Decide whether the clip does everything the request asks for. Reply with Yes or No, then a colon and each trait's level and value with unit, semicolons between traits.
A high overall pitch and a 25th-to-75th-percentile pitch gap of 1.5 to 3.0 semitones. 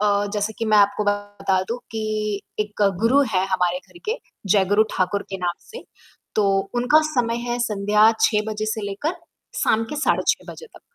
Yes: high, 210 Hz; narrow, 2.4 semitones